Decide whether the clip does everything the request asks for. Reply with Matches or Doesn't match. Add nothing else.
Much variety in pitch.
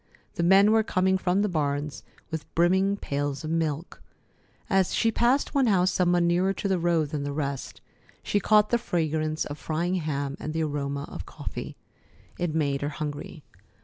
Doesn't match